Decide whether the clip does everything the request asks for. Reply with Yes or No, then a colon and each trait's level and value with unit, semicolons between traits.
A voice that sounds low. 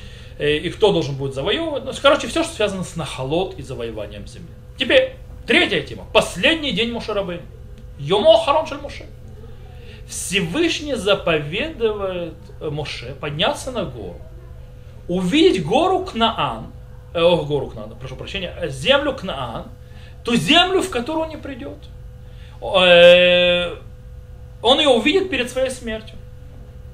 No: high, 195 Hz